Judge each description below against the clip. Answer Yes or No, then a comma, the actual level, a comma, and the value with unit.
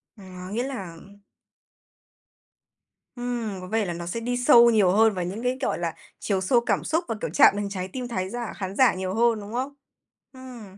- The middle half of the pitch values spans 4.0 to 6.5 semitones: Yes, average, 4.3 semitones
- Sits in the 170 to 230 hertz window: Yes, high, 220 Hz